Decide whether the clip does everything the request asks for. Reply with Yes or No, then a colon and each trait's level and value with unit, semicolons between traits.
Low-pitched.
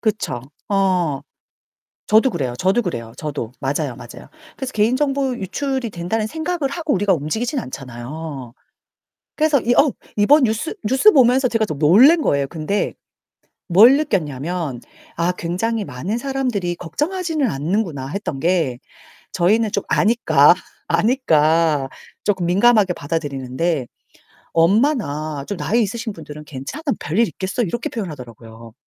No: medium, 185 Hz